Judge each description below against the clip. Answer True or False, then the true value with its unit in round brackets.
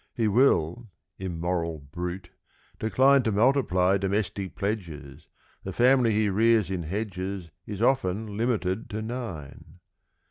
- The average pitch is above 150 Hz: False (100 Hz)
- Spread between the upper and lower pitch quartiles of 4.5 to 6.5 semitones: False (4.0 semitones)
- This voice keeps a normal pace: False (120 wpm)